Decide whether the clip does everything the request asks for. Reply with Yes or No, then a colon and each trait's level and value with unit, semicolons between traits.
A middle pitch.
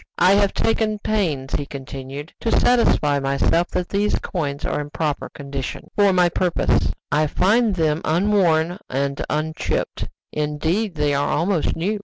Yes: medium, 160 Hz